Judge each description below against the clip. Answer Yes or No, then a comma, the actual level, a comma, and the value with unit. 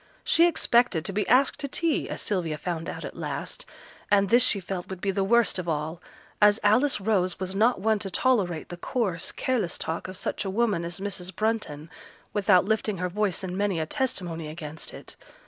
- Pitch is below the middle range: No, high, 195 Hz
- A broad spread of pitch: No, average, 3.9 semitones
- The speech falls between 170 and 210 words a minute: Yes, average, 200 wpm